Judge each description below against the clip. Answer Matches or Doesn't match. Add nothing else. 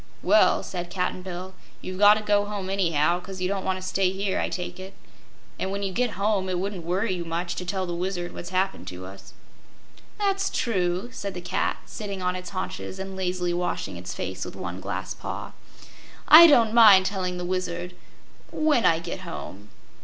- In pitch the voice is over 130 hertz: Matches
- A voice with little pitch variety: Matches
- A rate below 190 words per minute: Doesn't match